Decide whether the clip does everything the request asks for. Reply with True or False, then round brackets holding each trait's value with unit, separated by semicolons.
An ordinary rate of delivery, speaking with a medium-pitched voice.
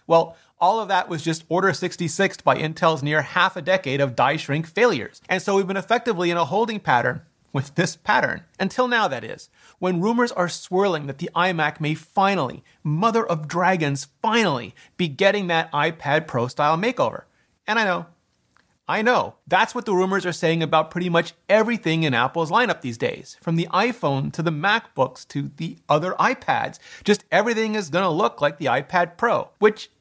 True (190 wpm; 175 Hz)